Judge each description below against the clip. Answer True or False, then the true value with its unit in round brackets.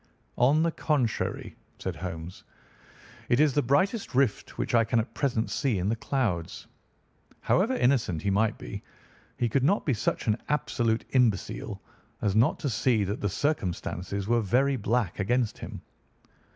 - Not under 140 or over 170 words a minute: True (160 wpm)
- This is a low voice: True (120 Hz)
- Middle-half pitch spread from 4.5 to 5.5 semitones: True (5.2 semitones)